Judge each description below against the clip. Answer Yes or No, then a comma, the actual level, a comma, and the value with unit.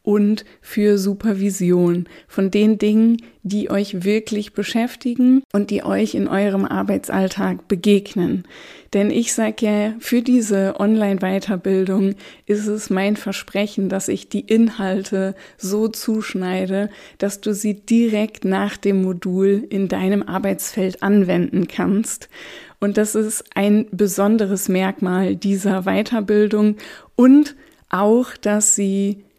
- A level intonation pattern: Yes, narrow, 1.8 semitones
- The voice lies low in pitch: No, high, 205 Hz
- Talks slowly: Yes, slow, 120 wpm